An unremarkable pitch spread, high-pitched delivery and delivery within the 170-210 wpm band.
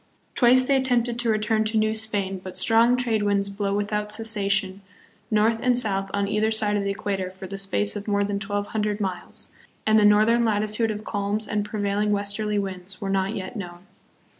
No: narrow, 1.7 semitones; high, 210 Hz; average, 195 wpm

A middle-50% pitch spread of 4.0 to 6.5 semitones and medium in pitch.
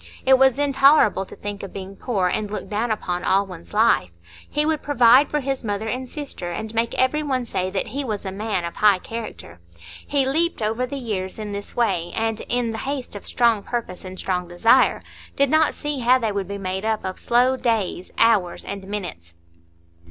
No: average, 5.0 semitones; high, 220 Hz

